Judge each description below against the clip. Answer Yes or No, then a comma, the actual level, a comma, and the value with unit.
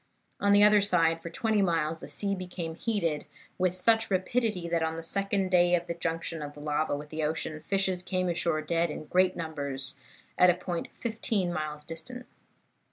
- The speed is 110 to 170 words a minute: No, average, 185 wpm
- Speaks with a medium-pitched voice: Yes, medium, 170 Hz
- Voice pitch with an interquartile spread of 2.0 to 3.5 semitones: Yes, average, 3.2 semitones